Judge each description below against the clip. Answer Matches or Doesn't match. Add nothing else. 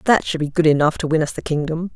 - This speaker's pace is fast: Matches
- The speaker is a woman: Matches